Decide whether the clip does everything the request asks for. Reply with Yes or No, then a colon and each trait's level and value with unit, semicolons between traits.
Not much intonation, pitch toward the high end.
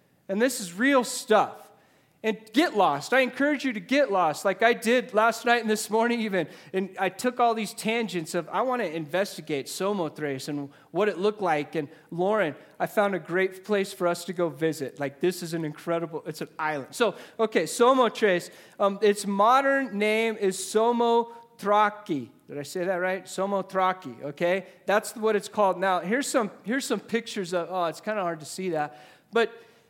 No: average, 4.8 semitones; high, 200 Hz